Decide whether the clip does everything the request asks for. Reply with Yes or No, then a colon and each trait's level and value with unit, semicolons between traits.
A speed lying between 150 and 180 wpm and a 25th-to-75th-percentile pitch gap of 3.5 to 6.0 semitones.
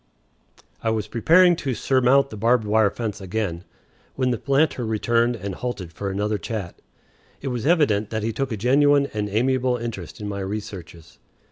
Yes: average, 170 wpm; average, 3.9 semitones